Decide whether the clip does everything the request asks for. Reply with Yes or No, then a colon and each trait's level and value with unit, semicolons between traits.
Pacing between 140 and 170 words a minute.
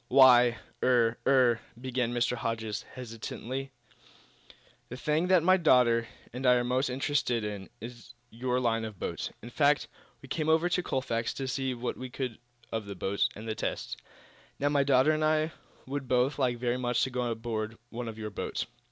No: average, 185 wpm